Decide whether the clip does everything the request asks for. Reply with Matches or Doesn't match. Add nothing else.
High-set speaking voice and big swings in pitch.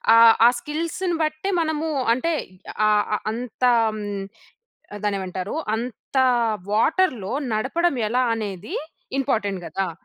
Matches